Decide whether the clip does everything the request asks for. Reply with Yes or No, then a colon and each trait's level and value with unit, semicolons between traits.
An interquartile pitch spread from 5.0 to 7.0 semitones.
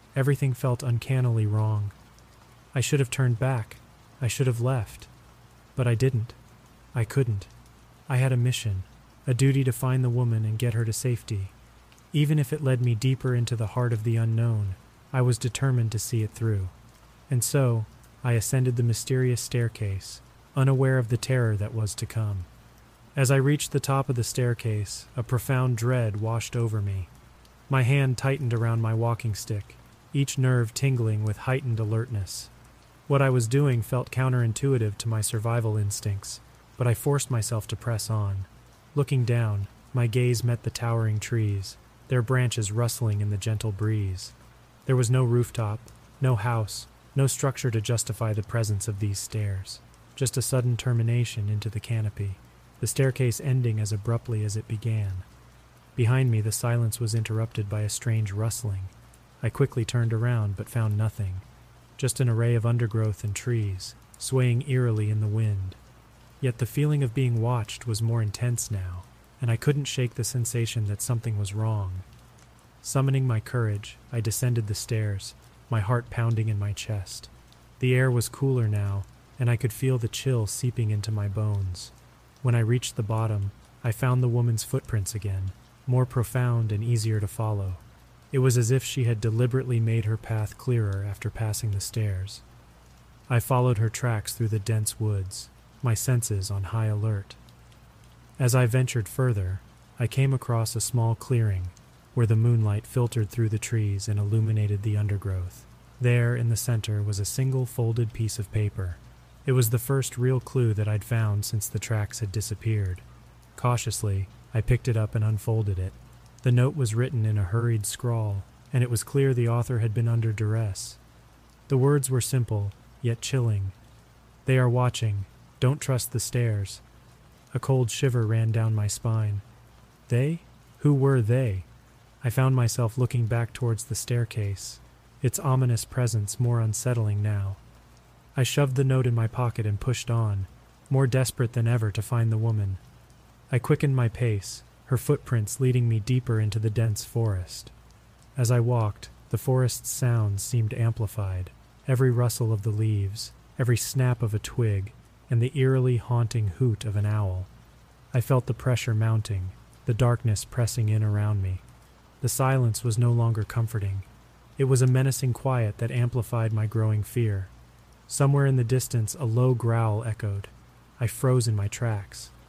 No: narrow, 2.6 semitones